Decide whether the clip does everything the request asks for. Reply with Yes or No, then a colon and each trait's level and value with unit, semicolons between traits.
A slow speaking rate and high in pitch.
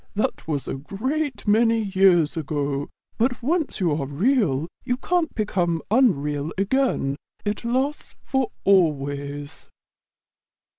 Yes: slow, 115 wpm; high, 195 Hz